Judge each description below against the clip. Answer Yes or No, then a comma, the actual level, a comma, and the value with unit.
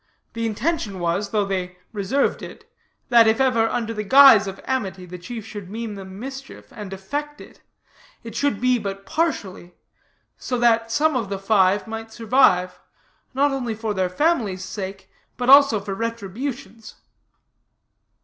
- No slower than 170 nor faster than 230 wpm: No, average, 155 wpm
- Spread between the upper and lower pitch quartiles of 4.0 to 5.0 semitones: Yes, average, 4.6 semitones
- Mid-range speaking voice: No, high, 225 Hz